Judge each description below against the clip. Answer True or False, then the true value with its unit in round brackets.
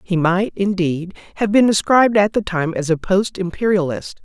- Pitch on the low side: False (190 Hz)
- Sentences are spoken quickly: False (185 wpm)